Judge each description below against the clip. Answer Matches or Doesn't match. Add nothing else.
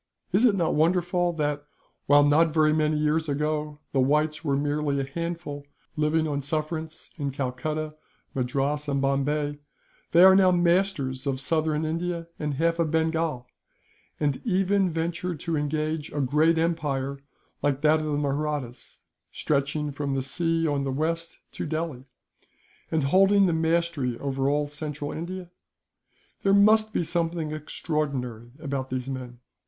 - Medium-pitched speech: Matches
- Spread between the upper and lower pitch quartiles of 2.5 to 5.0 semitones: Matches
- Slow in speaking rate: Doesn't match